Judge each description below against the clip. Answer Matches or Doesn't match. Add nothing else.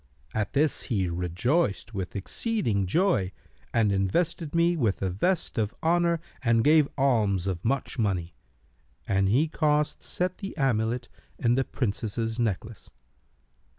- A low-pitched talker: Matches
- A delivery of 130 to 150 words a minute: Matches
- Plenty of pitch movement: Matches